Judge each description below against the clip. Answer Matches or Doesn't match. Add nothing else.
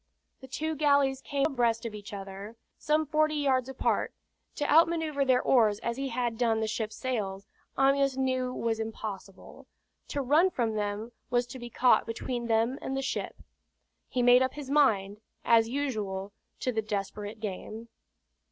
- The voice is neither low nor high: Doesn't match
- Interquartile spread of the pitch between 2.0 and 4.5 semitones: Matches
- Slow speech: Doesn't match